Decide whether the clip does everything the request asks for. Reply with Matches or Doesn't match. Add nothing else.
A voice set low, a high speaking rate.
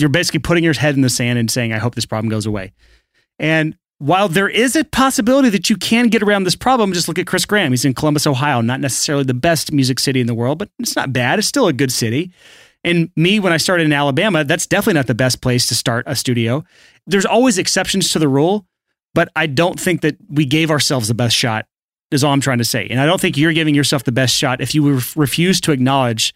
Doesn't match